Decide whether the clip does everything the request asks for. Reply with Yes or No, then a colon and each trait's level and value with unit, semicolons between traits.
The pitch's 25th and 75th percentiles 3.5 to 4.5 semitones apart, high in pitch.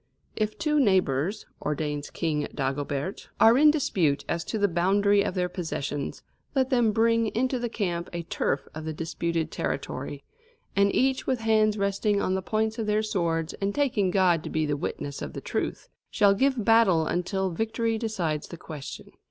No: wide, 5.5 semitones; high, 195 Hz